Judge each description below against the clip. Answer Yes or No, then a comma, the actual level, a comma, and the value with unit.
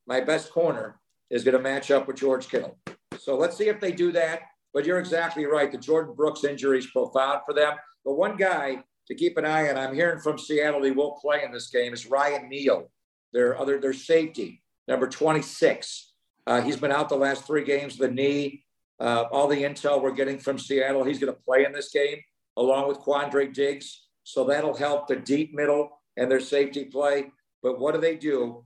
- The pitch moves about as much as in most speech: No, narrow, 1.9 semitones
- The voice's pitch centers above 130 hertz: Yes, medium, 140 Hz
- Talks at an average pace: No, fast, 210 wpm